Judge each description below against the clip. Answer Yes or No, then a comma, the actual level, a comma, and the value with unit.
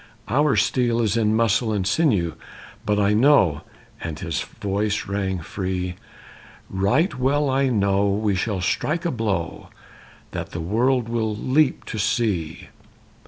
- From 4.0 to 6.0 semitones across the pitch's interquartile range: Yes, average, 4.3 semitones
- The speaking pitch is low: Yes, low, 105 Hz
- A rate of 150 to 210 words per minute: No, average, 140 wpm